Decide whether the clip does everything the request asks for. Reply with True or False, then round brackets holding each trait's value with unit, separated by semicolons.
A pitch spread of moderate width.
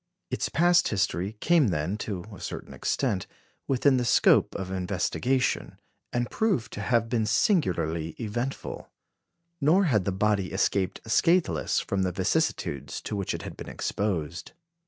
False (5.8 semitones)